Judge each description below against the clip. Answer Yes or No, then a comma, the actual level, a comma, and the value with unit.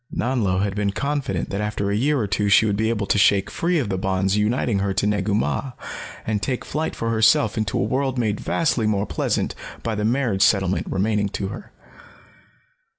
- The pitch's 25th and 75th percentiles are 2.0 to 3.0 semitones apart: Yes, average, 2.7 semitones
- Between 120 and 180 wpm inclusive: No, fast, 205 wpm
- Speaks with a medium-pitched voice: No, low, 105 Hz